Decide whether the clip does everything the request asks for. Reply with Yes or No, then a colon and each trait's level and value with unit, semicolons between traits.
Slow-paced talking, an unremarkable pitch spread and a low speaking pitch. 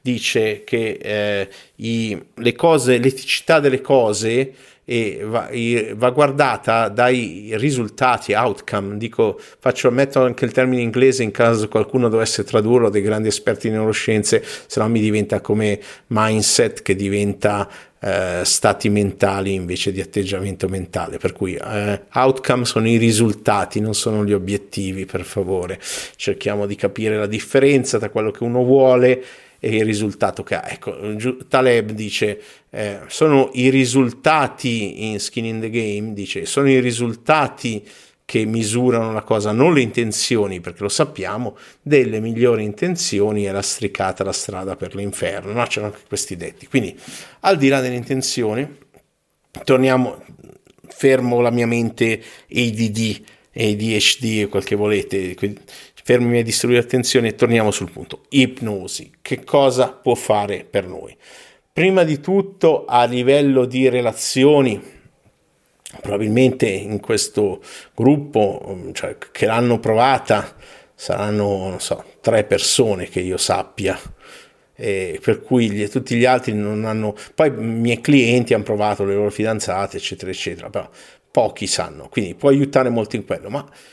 No: average, 145 wpm; average, 3.8 semitones; low, 115 Hz